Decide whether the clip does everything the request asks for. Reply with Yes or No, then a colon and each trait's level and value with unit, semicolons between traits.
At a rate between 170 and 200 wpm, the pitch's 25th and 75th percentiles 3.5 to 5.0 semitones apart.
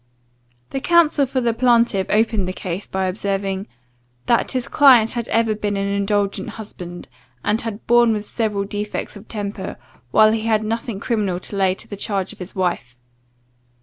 No: average, 175 wpm; average, 2.7 semitones